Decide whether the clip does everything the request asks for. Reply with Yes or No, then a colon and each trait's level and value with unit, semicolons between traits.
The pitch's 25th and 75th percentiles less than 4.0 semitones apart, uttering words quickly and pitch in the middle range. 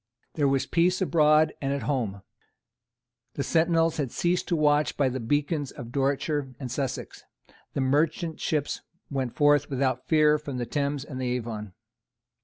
No: average, 2.7 semitones; average, 160 wpm; medium, 145 Hz